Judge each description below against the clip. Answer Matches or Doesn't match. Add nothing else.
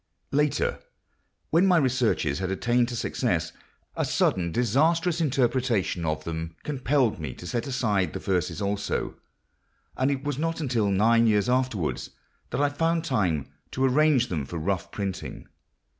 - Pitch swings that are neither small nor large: Doesn't match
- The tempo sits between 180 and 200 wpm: Doesn't match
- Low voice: Matches